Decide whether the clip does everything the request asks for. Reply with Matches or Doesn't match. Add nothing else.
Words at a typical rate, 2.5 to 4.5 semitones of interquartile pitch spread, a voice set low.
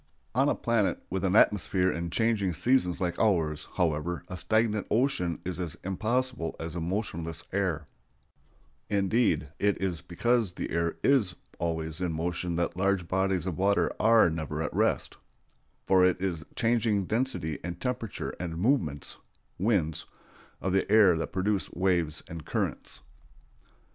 Matches